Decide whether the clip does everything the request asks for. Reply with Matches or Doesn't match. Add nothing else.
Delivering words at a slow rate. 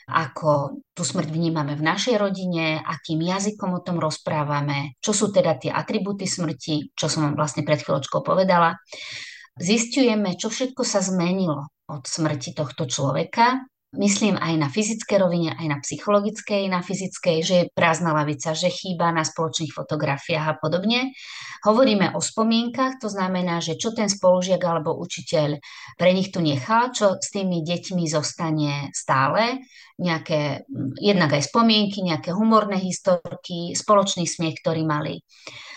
Doesn't match